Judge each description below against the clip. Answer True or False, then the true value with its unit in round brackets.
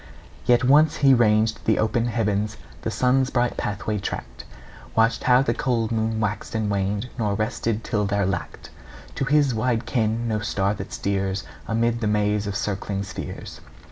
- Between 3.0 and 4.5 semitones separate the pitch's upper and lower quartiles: False (2.5 semitones)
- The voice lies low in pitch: True (110 Hz)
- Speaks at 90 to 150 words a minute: False (170 wpm)